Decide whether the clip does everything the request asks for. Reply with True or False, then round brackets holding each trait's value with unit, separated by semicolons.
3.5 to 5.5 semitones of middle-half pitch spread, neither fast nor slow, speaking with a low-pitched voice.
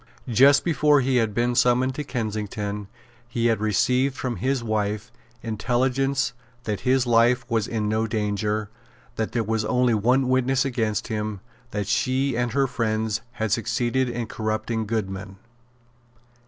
False (2.8 semitones; 145 wpm; 115 Hz)